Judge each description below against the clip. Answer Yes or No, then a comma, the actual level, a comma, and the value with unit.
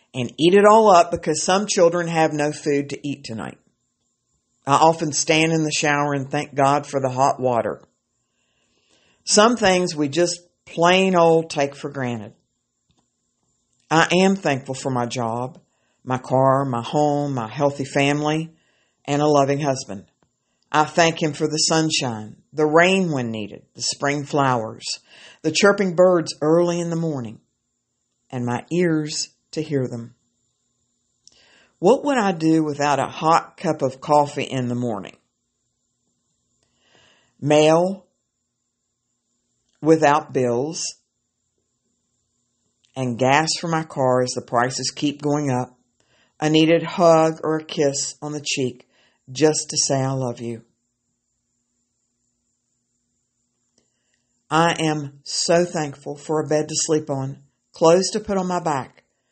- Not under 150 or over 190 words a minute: No, average, 140 wpm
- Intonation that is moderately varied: Yes, average, 4.5 semitones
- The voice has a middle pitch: Yes, medium, 145 Hz